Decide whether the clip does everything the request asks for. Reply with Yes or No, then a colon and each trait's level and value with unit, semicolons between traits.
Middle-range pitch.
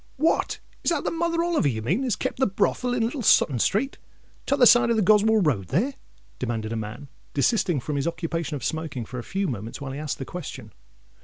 Yes: medium, 170 Hz